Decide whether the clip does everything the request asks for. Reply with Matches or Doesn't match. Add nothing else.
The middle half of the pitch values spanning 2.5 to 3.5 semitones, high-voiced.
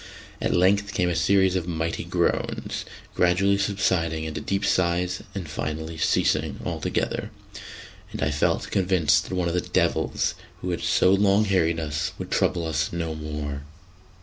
Doesn't match